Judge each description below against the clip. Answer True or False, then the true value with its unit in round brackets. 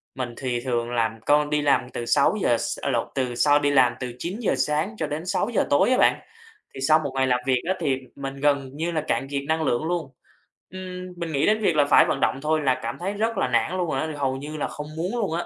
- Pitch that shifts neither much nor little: True (4.6 semitones)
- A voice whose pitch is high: False (145 Hz)